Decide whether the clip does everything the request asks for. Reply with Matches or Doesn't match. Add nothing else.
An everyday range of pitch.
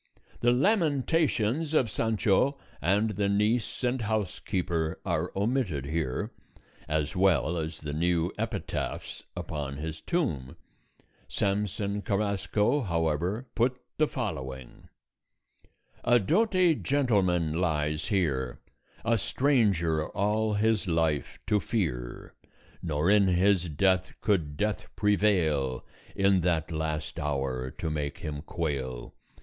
Doesn't match